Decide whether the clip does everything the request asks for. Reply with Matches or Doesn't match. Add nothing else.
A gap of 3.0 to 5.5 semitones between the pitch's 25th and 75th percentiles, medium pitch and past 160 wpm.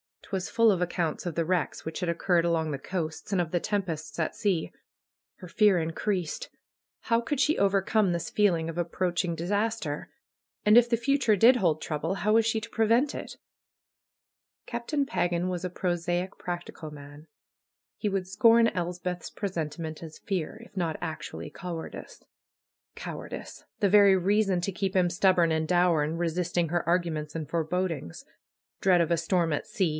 Matches